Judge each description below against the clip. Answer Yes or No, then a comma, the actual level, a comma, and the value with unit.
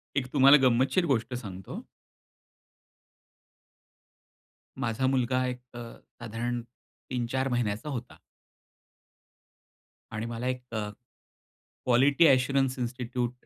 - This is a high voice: No, low, 125 Hz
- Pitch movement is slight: Yes, narrow, 1.9 semitones